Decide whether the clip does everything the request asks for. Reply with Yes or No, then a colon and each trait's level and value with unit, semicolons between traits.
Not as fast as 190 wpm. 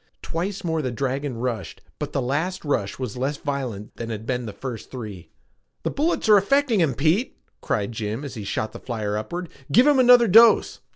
No: average, 195 wpm